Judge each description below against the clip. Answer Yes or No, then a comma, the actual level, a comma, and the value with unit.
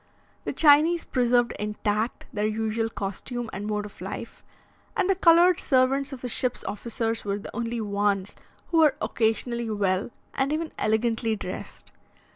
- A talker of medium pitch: No, high, 230 Hz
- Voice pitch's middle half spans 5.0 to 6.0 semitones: No, average, 4.2 semitones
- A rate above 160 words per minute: No, average, 150 wpm